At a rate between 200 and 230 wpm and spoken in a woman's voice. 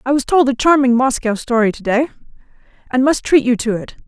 Yes: fast, 205 wpm; female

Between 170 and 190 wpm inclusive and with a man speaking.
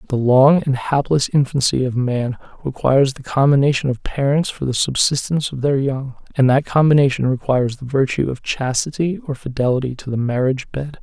Yes: average, 175 wpm; male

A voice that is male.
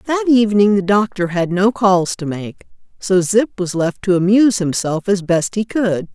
No: female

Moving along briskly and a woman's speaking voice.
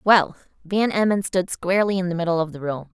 Yes: fast, 220 wpm; female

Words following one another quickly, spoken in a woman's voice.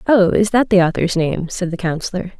Yes: fast, 225 wpm; female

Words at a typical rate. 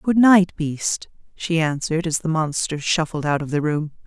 Yes: average, 190 wpm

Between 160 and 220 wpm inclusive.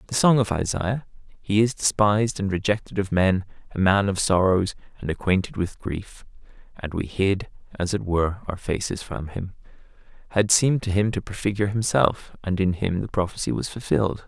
Yes: average, 180 wpm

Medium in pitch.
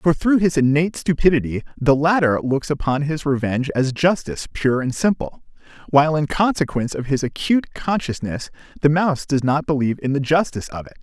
Yes: medium, 145 Hz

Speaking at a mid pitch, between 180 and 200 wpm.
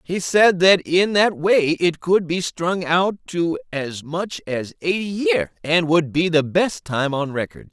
Yes: medium, 170 Hz; average, 195 wpm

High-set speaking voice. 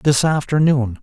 No: low, 135 Hz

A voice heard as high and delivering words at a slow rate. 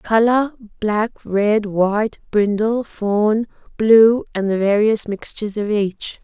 Yes: high, 215 Hz; slow, 115 wpm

